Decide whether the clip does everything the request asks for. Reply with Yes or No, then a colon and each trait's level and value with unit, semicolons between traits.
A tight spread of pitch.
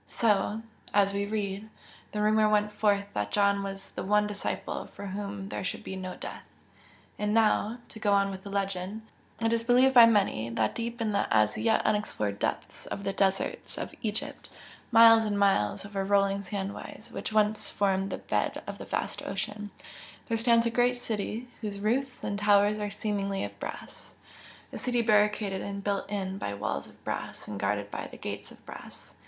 Yes: narrow, 1.8 semitones